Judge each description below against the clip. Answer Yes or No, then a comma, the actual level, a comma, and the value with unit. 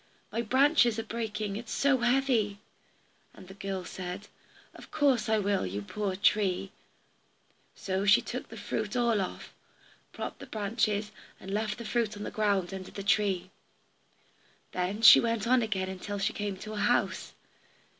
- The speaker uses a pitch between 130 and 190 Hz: No, high, 210 Hz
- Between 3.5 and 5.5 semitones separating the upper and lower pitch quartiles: No, average, 2.9 semitones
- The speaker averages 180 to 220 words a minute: No, average, 170 wpm